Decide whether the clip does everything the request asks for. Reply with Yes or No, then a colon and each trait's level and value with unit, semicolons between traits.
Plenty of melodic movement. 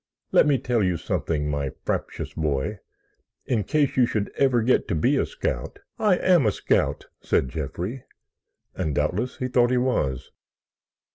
Yes: wide, 8.7 semitones